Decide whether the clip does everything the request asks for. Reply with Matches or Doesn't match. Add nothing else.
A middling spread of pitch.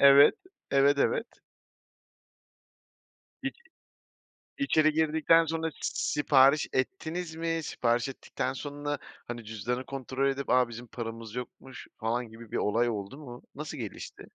Matches